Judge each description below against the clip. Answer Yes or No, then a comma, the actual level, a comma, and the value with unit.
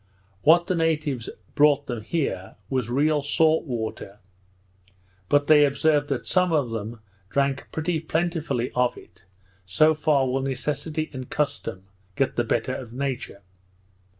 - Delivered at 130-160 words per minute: Yes, average, 140 wpm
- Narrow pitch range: No, average, 4.1 semitones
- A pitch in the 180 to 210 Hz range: No, medium, 140 Hz